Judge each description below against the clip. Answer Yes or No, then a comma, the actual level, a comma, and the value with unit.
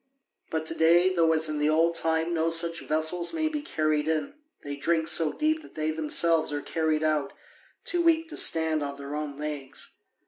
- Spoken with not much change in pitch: Yes, narrow, 1.7 semitones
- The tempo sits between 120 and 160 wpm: No, average, 200 wpm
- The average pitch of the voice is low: No, medium, 160 Hz